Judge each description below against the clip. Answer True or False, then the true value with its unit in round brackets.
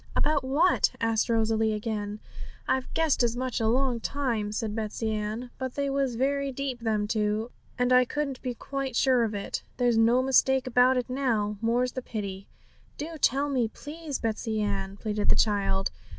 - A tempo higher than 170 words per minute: True (180 wpm)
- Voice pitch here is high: True (240 Hz)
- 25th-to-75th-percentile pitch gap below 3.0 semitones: False (3.5 semitones)